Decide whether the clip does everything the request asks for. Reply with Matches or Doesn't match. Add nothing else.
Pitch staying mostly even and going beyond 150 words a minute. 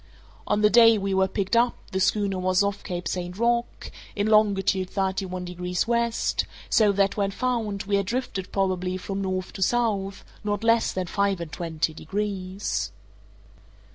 Matches